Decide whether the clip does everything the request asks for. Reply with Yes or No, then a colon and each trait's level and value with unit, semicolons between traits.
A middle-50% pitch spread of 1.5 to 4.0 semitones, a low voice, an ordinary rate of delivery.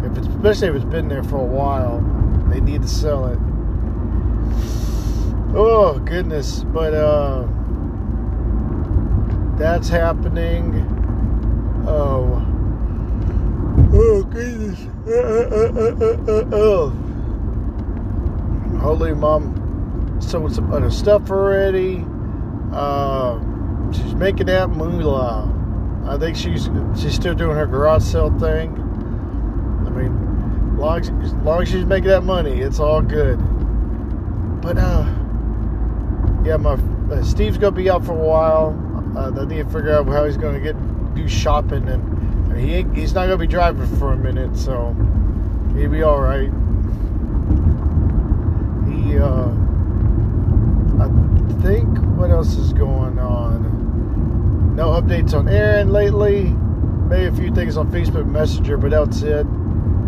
No: average, 3.7 semitones; low, 100 Hz; slow, 120 wpm